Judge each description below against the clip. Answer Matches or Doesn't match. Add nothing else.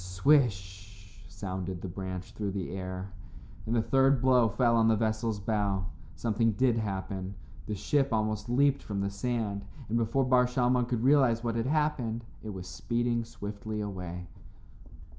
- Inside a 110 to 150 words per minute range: Doesn't match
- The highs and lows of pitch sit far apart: Doesn't match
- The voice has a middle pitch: Doesn't match